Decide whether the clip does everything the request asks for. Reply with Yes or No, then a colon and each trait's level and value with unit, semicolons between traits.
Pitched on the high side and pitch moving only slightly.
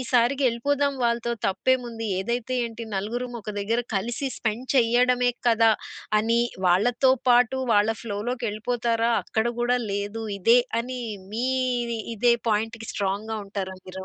Yes: high, 235 Hz; narrow, 2.2 semitones